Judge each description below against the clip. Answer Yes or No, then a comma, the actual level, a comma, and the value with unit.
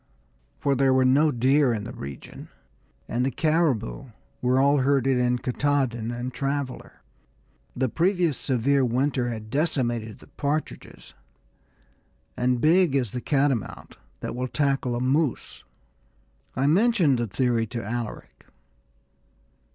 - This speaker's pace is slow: Yes, slow, 130 wpm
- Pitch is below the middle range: Yes, low, 130 Hz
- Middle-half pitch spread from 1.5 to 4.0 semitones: Yes, average, 3.0 semitones